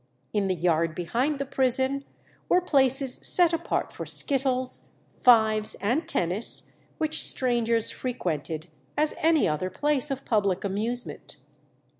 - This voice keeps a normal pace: No, slow, 125 wpm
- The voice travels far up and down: Yes, wide, 6.0 semitones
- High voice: Yes, high, 245 Hz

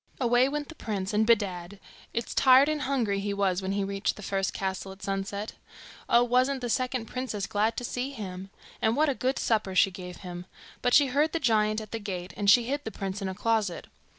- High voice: Yes, high, 215 Hz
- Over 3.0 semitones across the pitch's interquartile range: Yes, average, 4.4 semitones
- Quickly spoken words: Yes, fast, 225 wpm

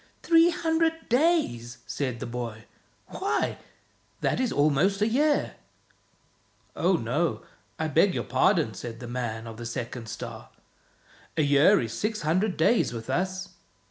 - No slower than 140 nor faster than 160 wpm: Yes, average, 150 wpm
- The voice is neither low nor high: Yes, medium, 155 Hz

